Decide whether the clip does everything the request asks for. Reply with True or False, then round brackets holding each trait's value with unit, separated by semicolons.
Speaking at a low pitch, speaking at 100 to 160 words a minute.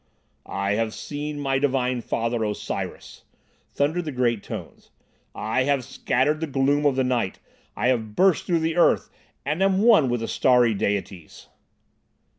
True (130 Hz; 155 wpm)